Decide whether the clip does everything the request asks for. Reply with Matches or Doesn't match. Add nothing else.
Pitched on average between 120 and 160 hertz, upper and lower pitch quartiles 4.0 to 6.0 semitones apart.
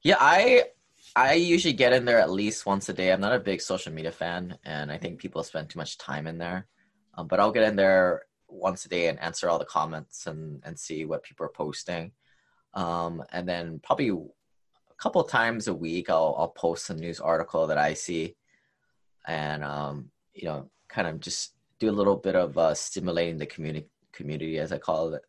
Doesn't match